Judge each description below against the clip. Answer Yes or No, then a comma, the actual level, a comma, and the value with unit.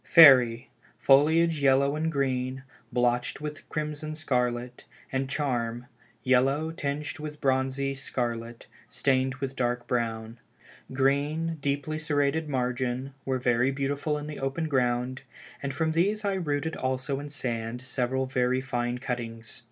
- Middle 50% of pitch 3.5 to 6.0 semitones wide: No, average, 3.0 semitones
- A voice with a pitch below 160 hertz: Yes, low, 135 Hz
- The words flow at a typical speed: No, slow, 130 wpm